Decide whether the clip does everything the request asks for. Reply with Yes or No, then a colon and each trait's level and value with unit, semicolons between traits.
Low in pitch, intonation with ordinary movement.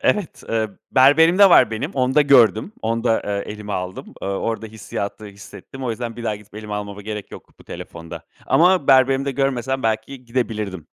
Yes: low, 115 Hz; average, 4.2 semitones